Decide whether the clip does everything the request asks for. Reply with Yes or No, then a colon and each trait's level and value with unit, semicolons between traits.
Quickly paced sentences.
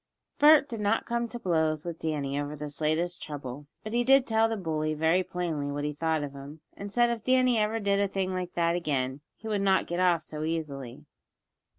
Yes: fast, 225 wpm